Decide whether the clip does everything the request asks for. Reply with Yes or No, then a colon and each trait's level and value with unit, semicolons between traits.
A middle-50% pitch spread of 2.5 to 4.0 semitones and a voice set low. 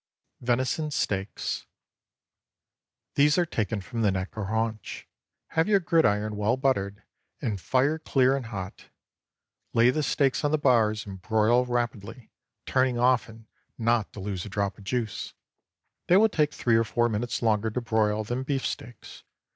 Yes: average, 3.7 semitones; low, 115 Hz